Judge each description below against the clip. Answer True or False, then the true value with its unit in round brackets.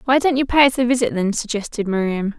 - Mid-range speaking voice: False (235 Hz)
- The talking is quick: True (250 wpm)